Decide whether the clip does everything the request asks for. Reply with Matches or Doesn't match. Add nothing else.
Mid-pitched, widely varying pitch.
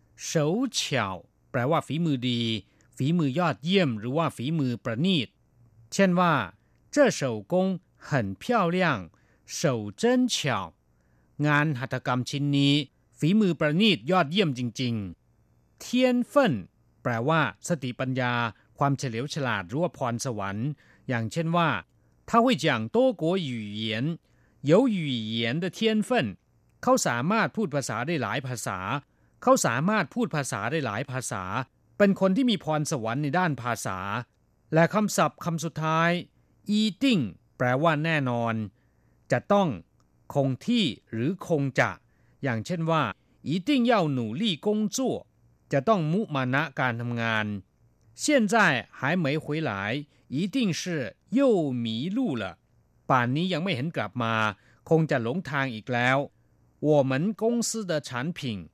Matches